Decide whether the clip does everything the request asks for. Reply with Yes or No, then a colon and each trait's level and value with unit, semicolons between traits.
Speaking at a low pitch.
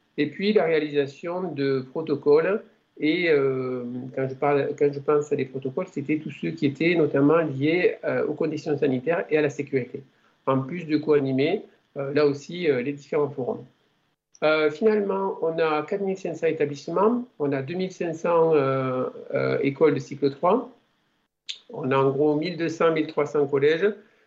No: medium, 150 Hz